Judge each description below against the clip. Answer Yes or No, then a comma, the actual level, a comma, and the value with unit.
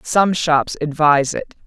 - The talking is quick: No, average, 145 wpm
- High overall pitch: No, medium, 155 Hz